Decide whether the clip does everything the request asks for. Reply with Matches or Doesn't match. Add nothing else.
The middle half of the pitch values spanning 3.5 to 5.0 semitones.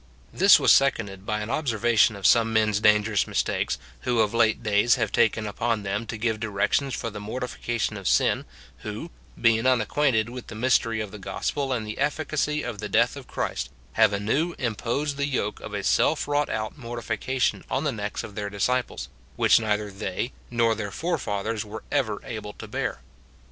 Doesn't match